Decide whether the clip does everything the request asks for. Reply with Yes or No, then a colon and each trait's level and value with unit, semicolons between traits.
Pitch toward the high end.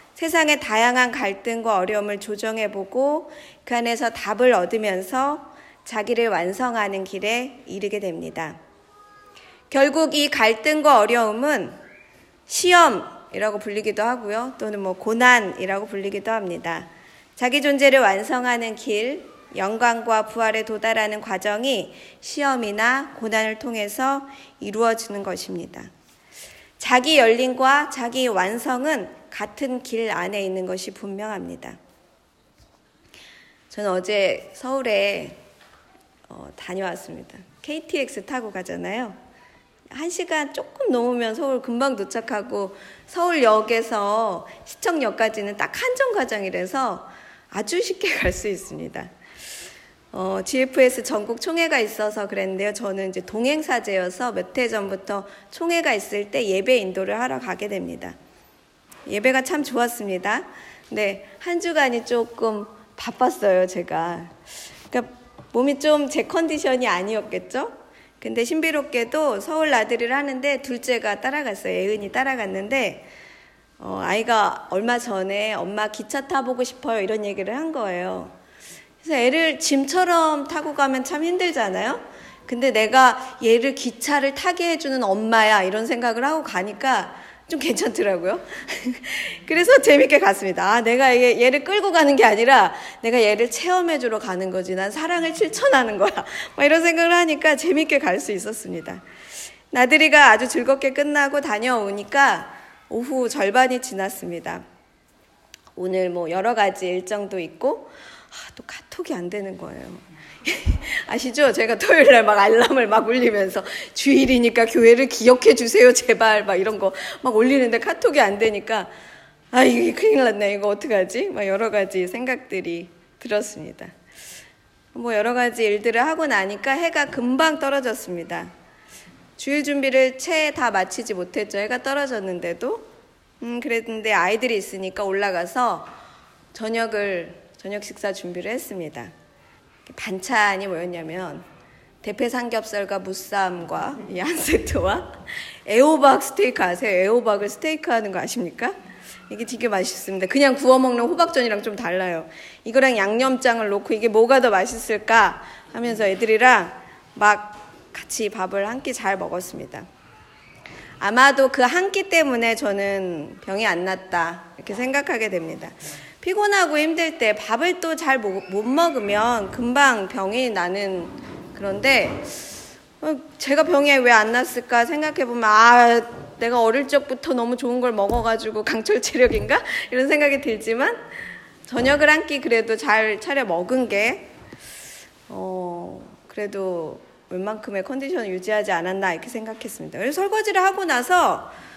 Yes: high, 235 Hz